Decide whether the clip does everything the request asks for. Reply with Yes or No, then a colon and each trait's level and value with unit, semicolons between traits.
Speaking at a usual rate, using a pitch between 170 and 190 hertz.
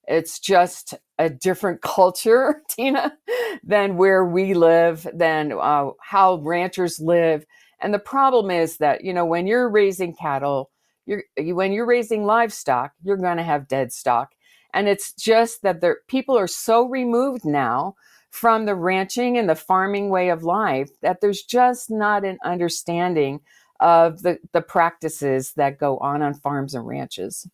Yes: average, 160 wpm; medium, 185 Hz